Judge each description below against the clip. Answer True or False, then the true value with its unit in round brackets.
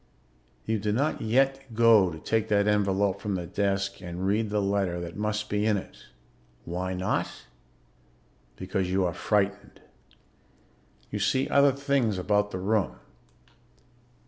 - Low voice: True (100 Hz)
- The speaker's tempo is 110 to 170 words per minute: True (145 wpm)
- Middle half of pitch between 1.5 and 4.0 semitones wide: True (2.7 semitones)